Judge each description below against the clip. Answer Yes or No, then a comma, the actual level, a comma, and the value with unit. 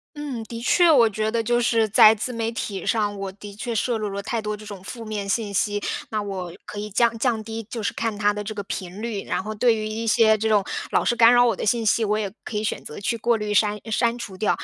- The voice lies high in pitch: Yes, high, 215 Hz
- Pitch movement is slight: Yes, narrow, 2.0 semitones